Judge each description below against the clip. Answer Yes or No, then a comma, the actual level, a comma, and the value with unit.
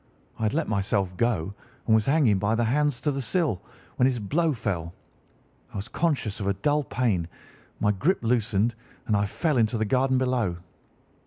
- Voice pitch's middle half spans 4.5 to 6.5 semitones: Yes, average, 4.9 semitones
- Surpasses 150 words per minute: Yes, average, 185 wpm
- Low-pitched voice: Yes, low, 115 Hz